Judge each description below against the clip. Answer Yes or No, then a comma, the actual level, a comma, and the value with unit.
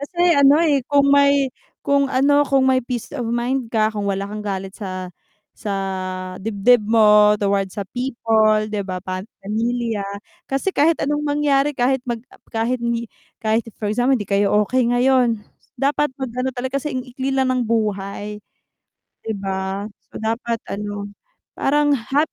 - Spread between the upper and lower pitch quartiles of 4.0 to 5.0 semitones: Yes, average, 4.4 semitones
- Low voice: No, high, 235 Hz